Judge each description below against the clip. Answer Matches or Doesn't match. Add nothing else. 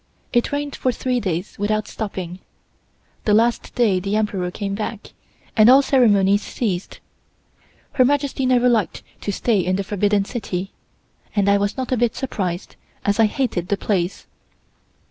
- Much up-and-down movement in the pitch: Doesn't match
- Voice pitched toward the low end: Doesn't match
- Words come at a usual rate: Matches